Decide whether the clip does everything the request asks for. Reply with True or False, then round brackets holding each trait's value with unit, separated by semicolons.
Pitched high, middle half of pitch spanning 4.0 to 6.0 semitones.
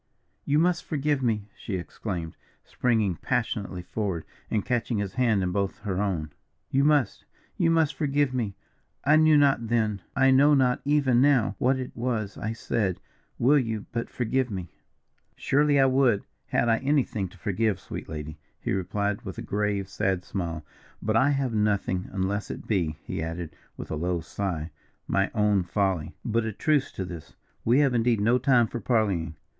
False (110 Hz; 5.4 semitones)